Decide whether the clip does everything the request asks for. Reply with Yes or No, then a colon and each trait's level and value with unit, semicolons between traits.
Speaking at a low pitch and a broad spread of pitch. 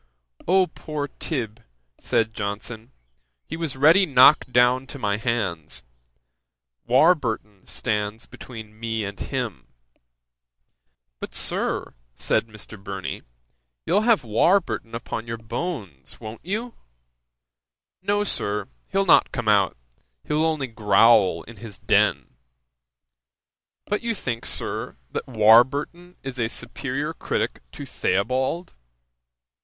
Yes: low, 115 Hz; wide, 6.1 semitones